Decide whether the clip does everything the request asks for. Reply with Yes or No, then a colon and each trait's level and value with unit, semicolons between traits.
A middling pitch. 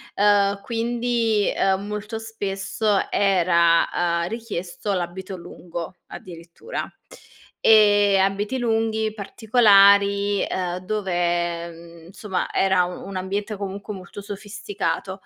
No: high, 200 Hz